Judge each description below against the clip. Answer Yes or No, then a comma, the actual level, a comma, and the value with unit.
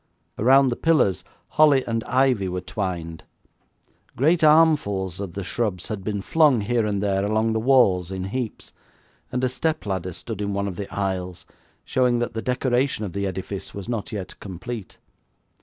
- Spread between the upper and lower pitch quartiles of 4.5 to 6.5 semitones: Yes, average, 4.8 semitones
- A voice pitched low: Yes, low, 105 Hz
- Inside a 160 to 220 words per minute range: Yes, average, 175 wpm